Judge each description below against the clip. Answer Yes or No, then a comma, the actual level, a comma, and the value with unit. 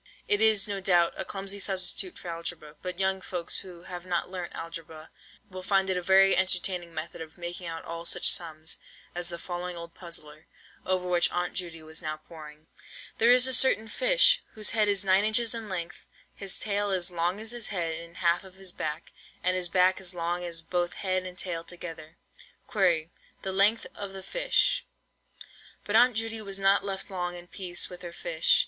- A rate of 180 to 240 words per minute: Yes, average, 200 wpm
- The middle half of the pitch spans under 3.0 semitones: Yes, narrow, 2.5 semitones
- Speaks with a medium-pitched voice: Yes, medium, 180 Hz